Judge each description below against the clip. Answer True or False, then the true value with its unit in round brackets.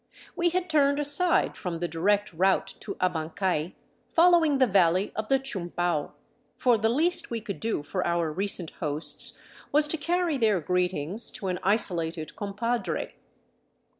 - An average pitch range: False (7.9 semitones)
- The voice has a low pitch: False (200 Hz)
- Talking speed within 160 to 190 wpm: False (150 wpm)